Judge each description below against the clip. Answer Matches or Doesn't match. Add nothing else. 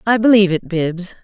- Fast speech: Doesn't match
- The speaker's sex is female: Matches